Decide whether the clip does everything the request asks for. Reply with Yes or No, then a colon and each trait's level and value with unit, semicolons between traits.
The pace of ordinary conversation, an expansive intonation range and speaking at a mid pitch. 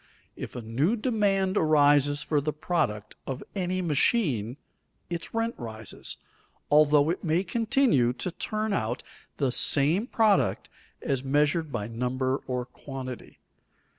No: slow, 130 wpm; wide, 6.5 semitones; medium, 150 Hz